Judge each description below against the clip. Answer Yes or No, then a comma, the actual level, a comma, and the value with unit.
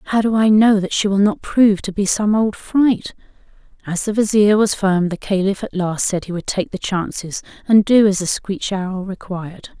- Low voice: No, high, 200 Hz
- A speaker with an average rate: No, fast, 220 wpm